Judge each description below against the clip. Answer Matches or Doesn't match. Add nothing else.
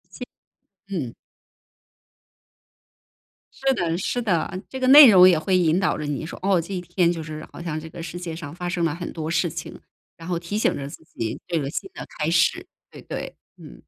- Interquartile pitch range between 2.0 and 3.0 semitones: Matches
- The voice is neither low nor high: Matches